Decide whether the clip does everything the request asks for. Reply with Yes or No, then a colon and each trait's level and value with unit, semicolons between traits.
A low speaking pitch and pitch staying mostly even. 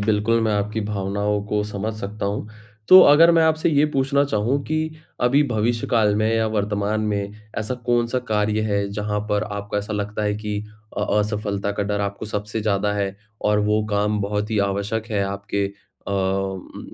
Yes: low, 105 Hz; narrow, 1.5 semitones